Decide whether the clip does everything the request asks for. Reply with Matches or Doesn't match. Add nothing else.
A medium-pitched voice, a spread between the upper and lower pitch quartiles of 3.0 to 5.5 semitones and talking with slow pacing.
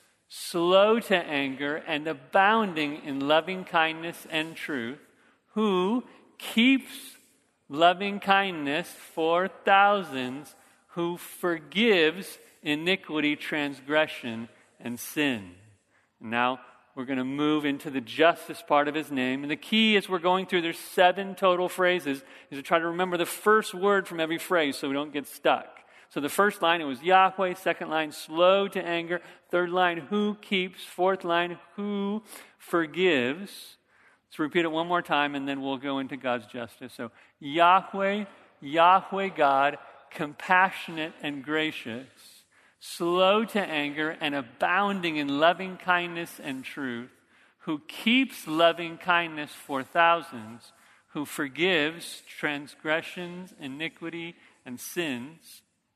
Matches